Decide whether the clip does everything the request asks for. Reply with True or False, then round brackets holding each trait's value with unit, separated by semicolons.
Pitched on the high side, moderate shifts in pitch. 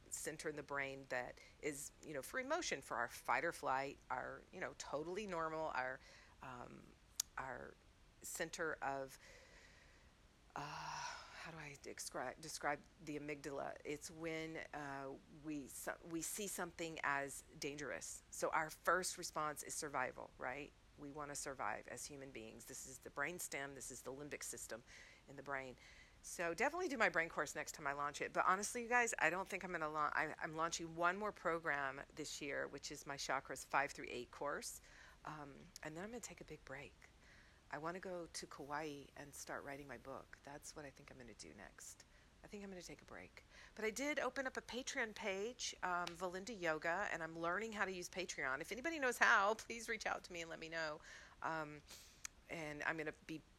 False (160 Hz; 4.6 semitones)